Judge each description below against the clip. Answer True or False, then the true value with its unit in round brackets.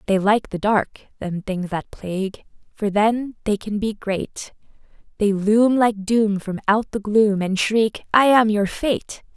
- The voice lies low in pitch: False (210 Hz)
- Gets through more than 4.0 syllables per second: False (3.8 syllables/s)